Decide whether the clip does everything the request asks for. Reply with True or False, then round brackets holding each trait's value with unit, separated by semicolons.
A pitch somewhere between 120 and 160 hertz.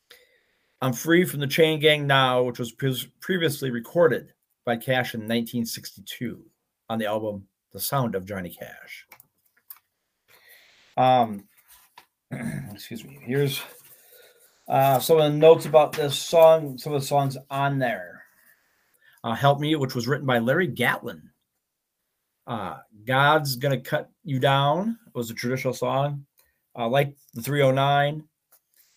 True (140 Hz)